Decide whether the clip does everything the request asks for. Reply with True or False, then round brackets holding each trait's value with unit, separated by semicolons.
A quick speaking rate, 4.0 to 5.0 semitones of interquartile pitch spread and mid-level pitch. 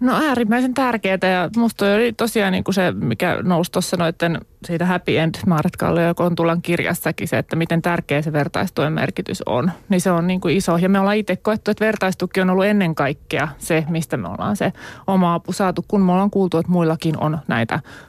False (200 wpm; 2.8 semitones; 180 Hz)